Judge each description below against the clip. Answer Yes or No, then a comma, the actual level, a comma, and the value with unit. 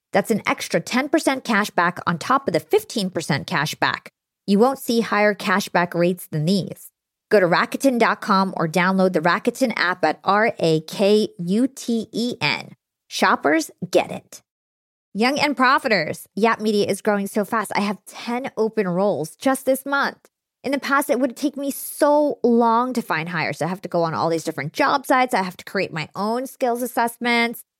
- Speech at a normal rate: Yes, average, 190 wpm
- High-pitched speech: Yes, high, 215 Hz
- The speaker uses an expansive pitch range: Yes, wide, 5.7 semitones